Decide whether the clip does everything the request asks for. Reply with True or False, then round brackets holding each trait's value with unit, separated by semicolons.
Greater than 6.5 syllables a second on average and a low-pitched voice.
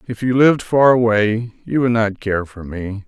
False (4.7 syllables/s; 115 Hz)